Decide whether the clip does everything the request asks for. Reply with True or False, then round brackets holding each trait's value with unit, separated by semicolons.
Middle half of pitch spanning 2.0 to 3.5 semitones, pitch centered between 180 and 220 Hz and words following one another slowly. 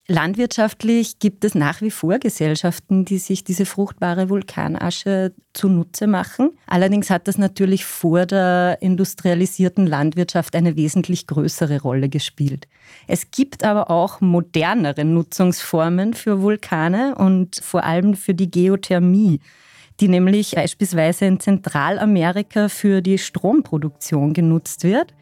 True (2.9 semitones; 185 Hz; 120 wpm)